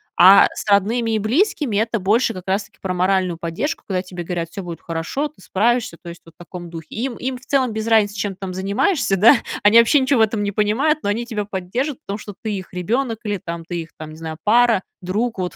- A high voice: Yes, high, 205 Hz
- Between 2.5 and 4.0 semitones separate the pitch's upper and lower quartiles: No, average, 4.4 semitones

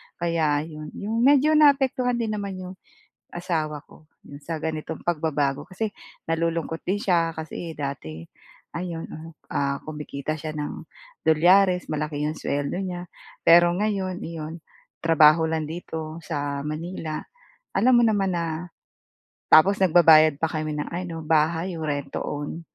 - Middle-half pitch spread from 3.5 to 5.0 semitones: No, average, 2.9 semitones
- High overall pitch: No, medium, 165 Hz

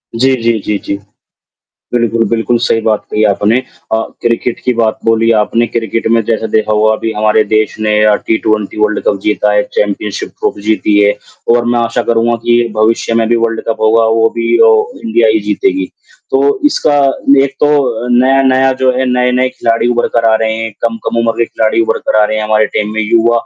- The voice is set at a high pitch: No, low, 115 Hz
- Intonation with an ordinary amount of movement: No, narrow, 1.6 semitones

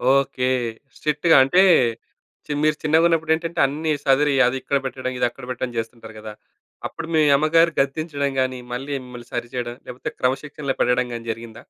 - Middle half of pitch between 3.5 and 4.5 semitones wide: Yes, average, 3.8 semitones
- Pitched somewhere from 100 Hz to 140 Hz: Yes, low, 135 Hz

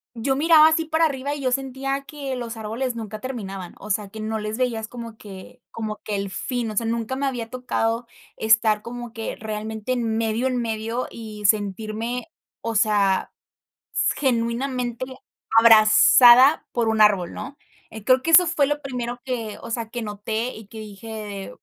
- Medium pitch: No, high, 230 Hz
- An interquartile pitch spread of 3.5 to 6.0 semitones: No, average, 3.0 semitones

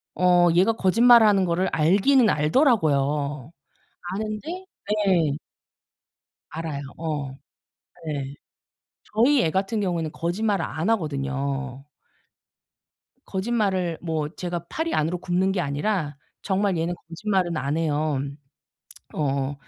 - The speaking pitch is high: No, medium, 175 Hz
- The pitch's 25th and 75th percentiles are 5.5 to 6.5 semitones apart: No, average, 5.1 semitones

